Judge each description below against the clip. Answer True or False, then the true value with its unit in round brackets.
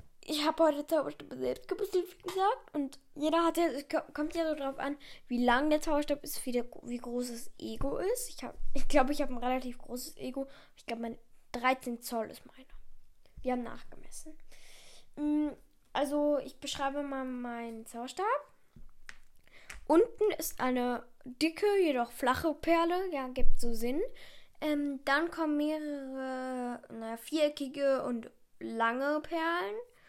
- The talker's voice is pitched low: False (285 Hz)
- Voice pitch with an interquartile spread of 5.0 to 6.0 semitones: False (4.2 semitones)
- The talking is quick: False (150 wpm)